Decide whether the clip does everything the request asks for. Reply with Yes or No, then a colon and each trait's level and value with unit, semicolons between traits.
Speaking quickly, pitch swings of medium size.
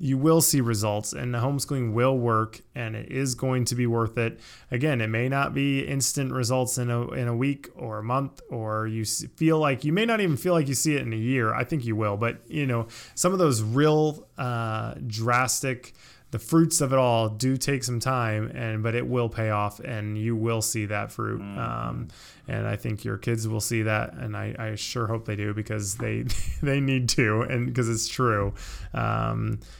Yes: fast, 220 wpm; average, 3.3 semitones